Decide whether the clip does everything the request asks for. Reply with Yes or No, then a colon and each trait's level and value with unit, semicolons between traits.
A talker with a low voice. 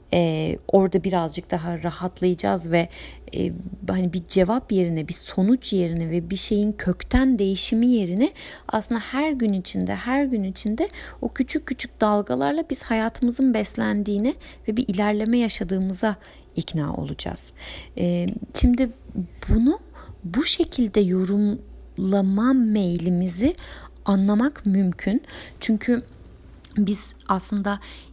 No: high, 205 Hz